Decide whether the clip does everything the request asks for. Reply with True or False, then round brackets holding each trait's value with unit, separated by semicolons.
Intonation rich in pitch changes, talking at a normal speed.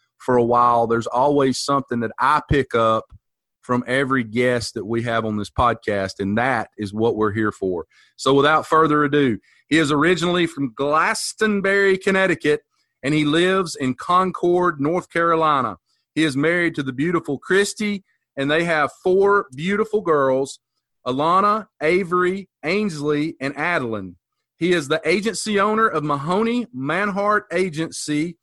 True (6.0 semitones; 150 wpm)